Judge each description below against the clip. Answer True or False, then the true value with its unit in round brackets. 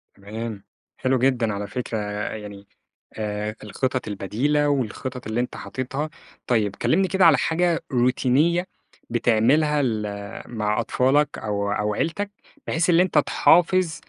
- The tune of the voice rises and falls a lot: True (5.7 semitones)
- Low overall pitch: True (125 Hz)